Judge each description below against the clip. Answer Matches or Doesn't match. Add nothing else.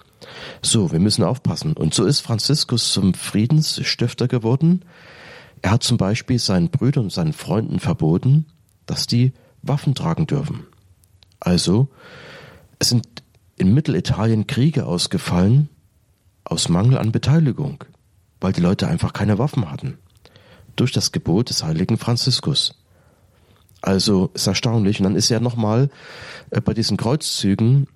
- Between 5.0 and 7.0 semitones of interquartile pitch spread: Matches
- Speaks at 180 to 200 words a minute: Doesn't match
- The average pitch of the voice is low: Matches